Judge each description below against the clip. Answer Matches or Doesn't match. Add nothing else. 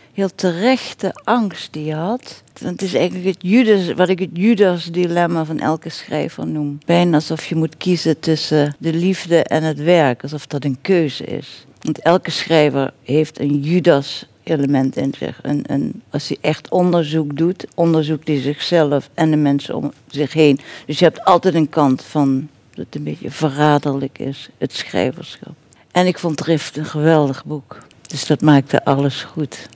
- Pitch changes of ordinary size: Matches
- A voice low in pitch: Doesn't match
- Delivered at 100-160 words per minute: Doesn't match